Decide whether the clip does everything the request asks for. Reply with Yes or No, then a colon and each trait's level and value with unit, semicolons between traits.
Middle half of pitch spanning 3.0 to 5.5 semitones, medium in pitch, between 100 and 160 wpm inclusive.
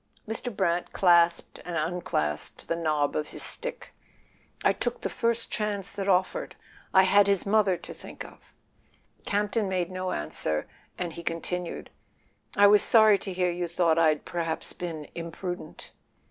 Yes: average, 3.3 semitones; medium, 180 Hz; average, 155 wpm